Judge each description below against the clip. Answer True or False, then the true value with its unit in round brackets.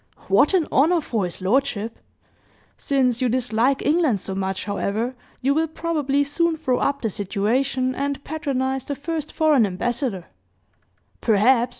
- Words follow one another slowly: False (150 wpm)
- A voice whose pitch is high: True (260 Hz)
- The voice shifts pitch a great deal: False (4.4 semitones)